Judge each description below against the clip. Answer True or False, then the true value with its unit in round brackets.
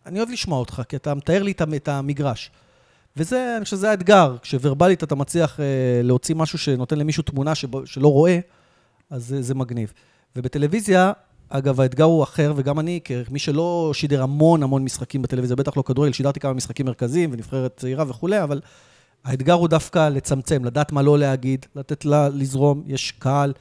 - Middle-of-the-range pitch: True (145 Hz)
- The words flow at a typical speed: False (170 wpm)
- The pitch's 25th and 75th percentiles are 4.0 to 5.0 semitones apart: False (3.2 semitones)